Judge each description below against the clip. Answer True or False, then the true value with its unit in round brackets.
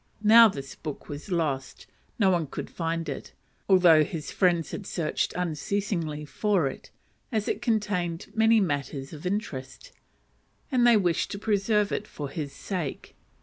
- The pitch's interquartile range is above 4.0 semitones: True (5.4 semitones)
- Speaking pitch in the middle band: True (175 Hz)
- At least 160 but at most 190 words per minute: False (150 wpm)